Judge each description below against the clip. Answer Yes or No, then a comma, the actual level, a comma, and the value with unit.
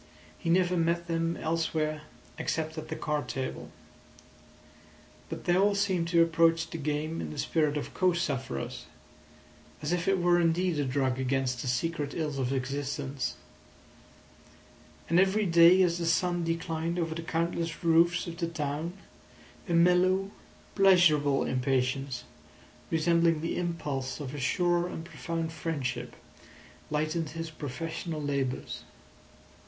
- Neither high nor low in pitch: Yes, medium, 165 Hz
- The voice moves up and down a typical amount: Yes, average, 3.0 semitones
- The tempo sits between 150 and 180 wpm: No, slow, 135 wpm